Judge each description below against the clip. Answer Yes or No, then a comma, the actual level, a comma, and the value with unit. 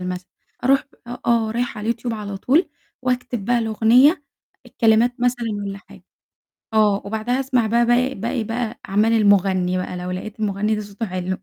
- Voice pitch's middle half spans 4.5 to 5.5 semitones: No, average, 3.3 semitones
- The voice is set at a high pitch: Yes, high, 220 Hz